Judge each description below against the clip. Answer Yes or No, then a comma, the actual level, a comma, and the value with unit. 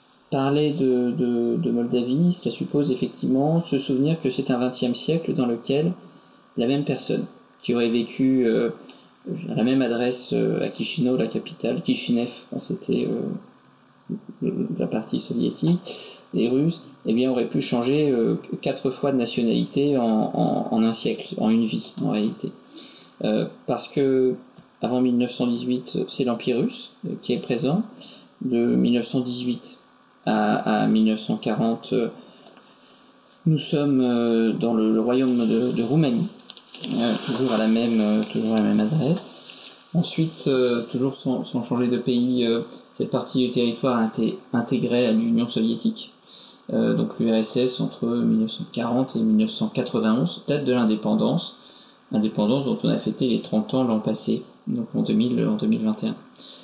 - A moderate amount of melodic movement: No, wide, 6.8 semitones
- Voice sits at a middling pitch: No, low, 130 Hz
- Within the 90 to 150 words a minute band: Yes, slow, 145 wpm